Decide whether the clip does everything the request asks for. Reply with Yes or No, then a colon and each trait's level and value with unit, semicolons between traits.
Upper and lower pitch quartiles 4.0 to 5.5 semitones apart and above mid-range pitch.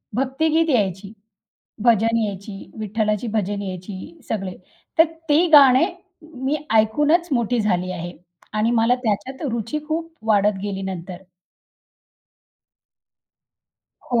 Yes: average, 5.2 semitones; high, 220 Hz